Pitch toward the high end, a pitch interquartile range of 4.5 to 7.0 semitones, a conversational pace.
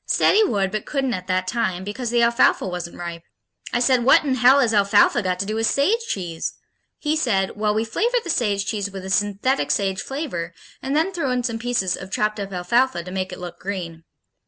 No: high, 210 Hz; average, 5.1 semitones; fast, 225 wpm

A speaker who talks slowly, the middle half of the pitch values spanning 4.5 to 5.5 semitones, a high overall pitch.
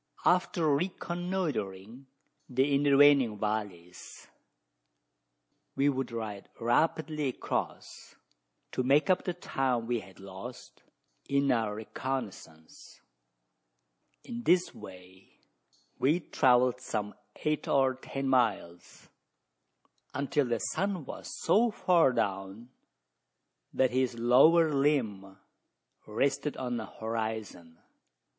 No: slow, 100 wpm; average, 5.2 semitones; low, 125 Hz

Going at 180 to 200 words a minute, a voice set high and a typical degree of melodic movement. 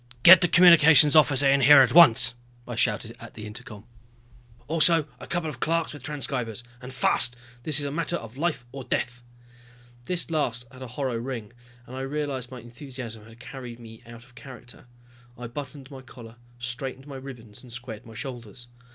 No: average, 185 wpm; low, 130 Hz; average, 3.5 semitones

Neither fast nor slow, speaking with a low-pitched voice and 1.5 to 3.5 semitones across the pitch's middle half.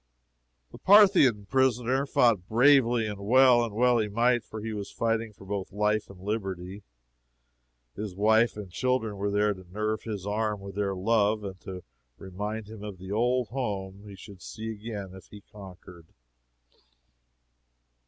Yes: average, 160 wpm; low, 105 Hz; average, 2.8 semitones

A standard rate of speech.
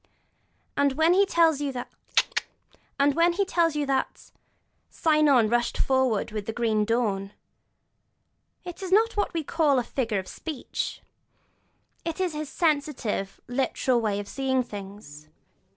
No: slow, 120 wpm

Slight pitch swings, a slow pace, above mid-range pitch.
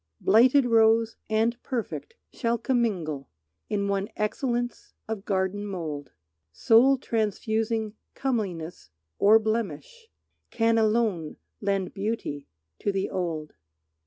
No: average, 3.3 semitones; slow, 100 wpm; high, 215 Hz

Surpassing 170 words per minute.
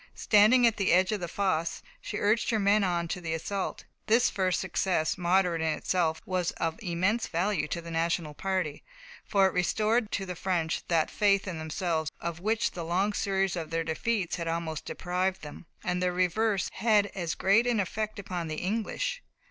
Yes: average, 190 wpm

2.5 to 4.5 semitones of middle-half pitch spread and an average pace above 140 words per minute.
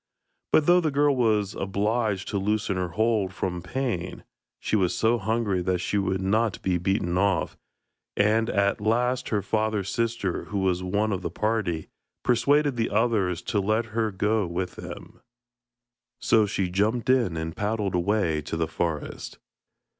Yes: average, 3.4 semitones; average, 160 wpm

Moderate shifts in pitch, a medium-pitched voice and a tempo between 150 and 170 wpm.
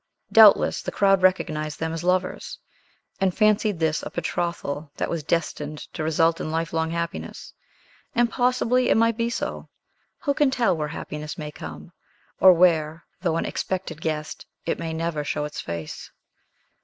Yes: average, 4.1 semitones; medium, 165 Hz; average, 160 wpm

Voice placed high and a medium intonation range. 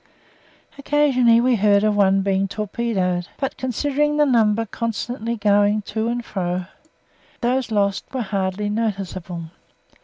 Yes: high, 215 Hz; average, 3.5 semitones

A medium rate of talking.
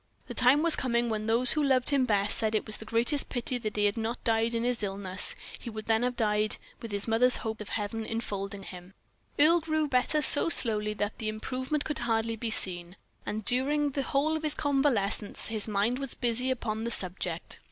No: fast, 215 wpm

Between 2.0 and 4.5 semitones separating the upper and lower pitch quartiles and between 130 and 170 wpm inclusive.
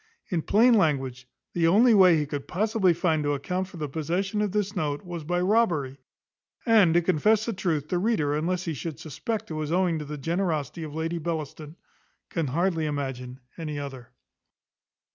No: average, 4.1 semitones; average, 180 wpm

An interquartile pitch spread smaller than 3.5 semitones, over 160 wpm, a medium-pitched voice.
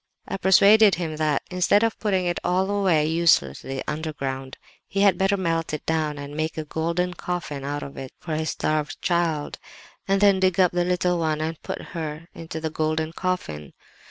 Yes: average, 3.0 semitones; average, 185 wpm; medium, 165 Hz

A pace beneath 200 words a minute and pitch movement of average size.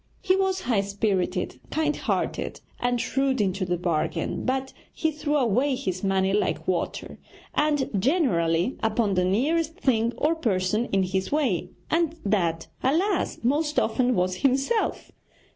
No: average, 145 wpm; wide, 7.7 semitones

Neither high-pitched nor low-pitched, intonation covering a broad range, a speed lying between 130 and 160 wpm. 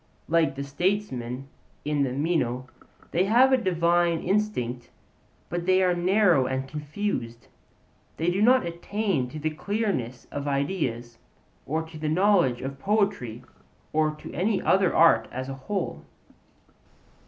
Yes: medium, 160 Hz; wide, 6.3 semitones; average, 140 wpm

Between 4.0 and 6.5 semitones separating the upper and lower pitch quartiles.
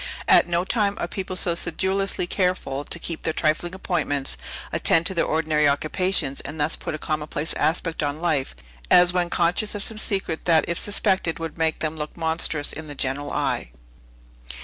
No: average, 2.9 semitones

